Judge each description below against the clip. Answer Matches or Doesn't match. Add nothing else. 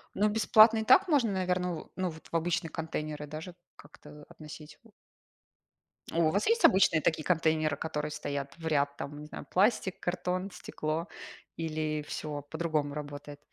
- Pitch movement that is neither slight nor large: Matches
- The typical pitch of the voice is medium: Matches